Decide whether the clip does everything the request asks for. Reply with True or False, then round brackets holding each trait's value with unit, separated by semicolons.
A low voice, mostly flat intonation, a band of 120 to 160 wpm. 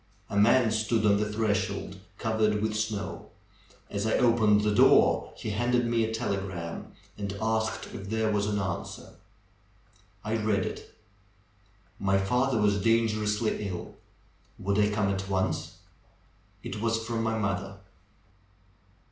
True (105 Hz; 2.0 semitones; 140 wpm)